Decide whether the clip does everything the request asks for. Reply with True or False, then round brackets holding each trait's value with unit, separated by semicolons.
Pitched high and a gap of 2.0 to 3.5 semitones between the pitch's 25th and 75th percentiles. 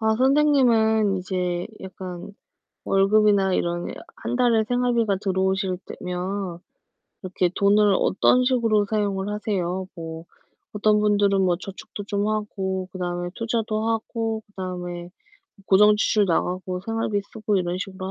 True (200 Hz; 2.8 semitones)